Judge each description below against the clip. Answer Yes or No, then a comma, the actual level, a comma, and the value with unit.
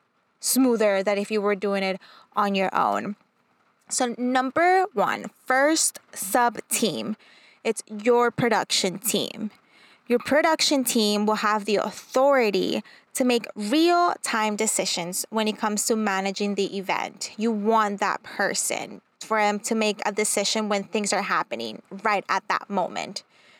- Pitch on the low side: No, high, 215 Hz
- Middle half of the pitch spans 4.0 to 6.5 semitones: No, average, 3.0 semitones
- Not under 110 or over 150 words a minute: Yes, average, 145 wpm